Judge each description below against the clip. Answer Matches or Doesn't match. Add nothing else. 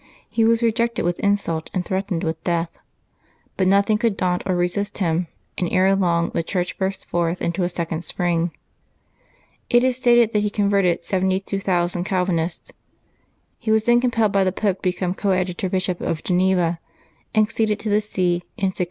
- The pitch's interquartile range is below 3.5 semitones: Matches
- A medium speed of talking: Matches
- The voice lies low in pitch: Doesn't match